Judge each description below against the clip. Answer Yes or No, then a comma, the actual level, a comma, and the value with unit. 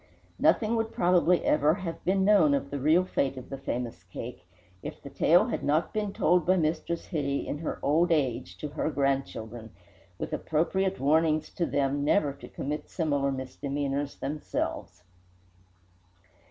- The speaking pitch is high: No, medium, 150 Hz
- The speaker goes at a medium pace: Yes, average, 155 wpm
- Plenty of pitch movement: No, average, 3.9 semitones